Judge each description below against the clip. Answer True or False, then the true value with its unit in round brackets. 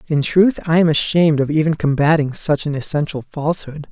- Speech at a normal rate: True (185 wpm)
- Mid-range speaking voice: True (155 Hz)